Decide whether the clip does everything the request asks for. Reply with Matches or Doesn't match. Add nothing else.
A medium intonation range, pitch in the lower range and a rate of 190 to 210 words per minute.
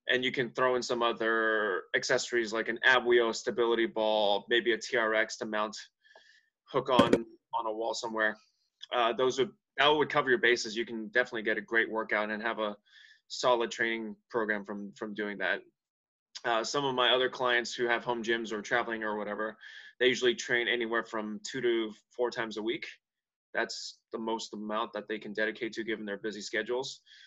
Doesn't match